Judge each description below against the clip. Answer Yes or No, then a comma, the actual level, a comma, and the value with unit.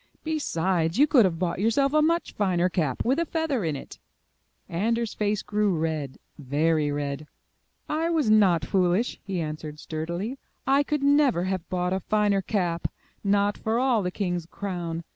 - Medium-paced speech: Yes, average, 165 wpm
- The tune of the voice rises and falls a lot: Yes, wide, 5.9 semitones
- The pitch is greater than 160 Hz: Yes, high, 190 Hz